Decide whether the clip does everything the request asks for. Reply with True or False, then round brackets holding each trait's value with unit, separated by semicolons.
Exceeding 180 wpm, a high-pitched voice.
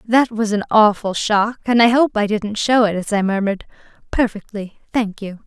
True (200 wpm; 215 Hz)